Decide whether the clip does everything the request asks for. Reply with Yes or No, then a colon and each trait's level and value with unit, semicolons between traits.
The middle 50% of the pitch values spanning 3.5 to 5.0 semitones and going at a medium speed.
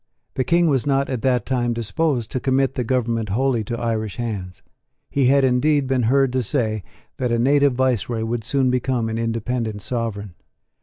No: average, 2.7 semitones; average, 185 wpm